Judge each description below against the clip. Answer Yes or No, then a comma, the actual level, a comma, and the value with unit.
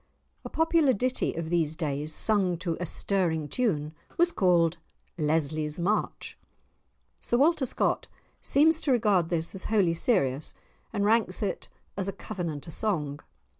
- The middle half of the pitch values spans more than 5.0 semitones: Yes, wide, 5.6 semitones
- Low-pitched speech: No, medium, 180 Hz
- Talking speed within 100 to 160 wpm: Yes, average, 140 wpm